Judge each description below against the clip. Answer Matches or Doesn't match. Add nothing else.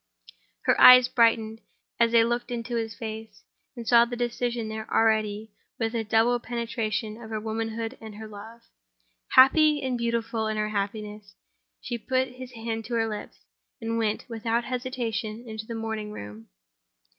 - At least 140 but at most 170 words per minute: Matches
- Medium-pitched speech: Doesn't match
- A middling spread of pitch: Doesn't match